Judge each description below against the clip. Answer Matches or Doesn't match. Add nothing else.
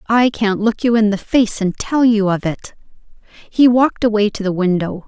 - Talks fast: Matches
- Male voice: Doesn't match